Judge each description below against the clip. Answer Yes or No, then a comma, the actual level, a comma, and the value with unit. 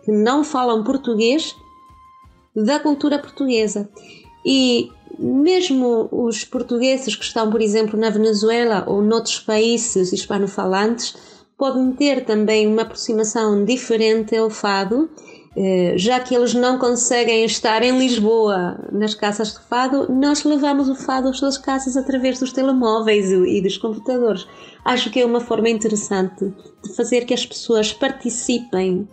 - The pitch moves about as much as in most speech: Yes, average, 3.2 semitones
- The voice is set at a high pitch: Yes, high, 230 Hz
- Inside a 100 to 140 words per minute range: Yes, average, 135 wpm